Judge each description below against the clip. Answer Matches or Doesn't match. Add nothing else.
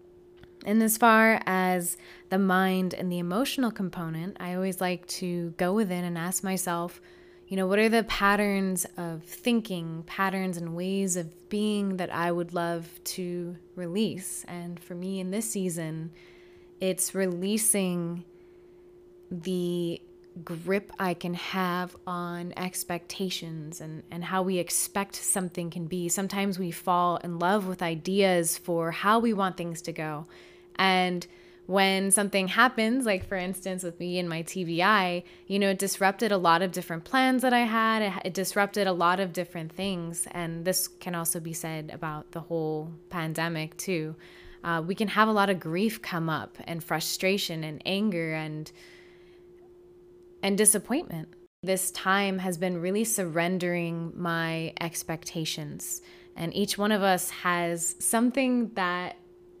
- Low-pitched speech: Doesn't match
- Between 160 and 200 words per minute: Doesn't match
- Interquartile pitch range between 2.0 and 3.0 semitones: Matches